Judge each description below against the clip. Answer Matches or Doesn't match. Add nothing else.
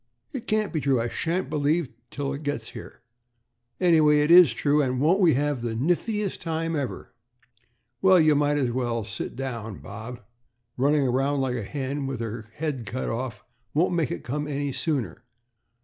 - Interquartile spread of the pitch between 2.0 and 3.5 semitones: Doesn't match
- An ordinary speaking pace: Matches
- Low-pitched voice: Doesn't match